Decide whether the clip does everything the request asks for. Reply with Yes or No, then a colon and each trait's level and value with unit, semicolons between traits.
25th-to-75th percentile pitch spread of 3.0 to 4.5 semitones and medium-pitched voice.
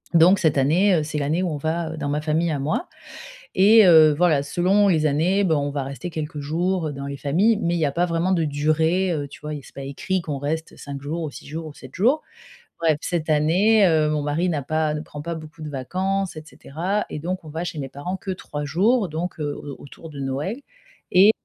Yes: average, 3.4 semitones; medium, 160 Hz